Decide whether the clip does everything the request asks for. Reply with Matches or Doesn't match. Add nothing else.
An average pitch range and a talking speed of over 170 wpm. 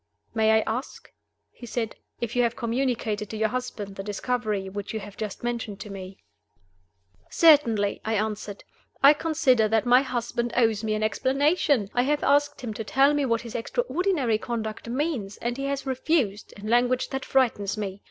Matches